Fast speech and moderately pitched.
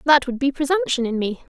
No: fast, 230 wpm; very high, 275 Hz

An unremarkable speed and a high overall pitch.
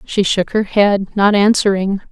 Yes: average, 170 wpm; high, 200 Hz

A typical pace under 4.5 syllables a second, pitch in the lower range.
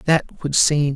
No: 3.1 syllables/s; medium, 145 Hz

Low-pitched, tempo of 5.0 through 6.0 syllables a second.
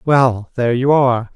Yes: low, 125 Hz; 5.1 syllables/s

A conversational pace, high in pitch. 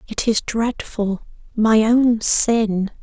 No: slow, 120 wpm; high, 220 Hz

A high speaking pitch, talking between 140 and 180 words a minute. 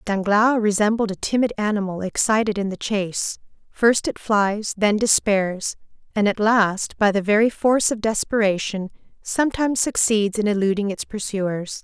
Yes: high, 210 Hz; average, 145 wpm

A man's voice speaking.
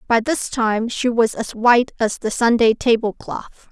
No: female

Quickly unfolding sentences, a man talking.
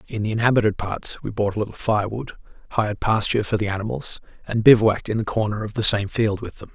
Yes: fast, 220 wpm; male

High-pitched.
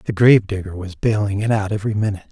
No: low, 105 Hz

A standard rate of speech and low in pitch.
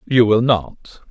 Yes: average, 165 wpm; low, 115 Hz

